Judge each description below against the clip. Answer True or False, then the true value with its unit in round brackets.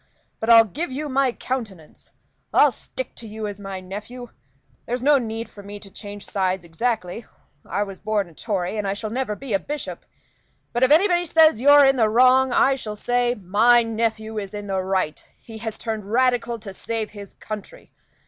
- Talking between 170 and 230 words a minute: True (195 wpm)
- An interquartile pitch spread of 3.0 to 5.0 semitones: True (3.5 semitones)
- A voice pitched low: False (220 Hz)